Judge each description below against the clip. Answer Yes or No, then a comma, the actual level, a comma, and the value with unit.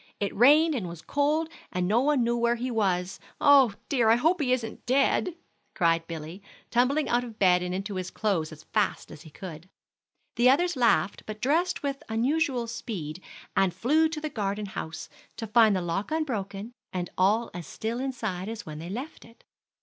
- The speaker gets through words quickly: No, average, 190 wpm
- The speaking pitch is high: Yes, high, 225 Hz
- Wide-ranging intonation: Yes, wide, 6.1 semitones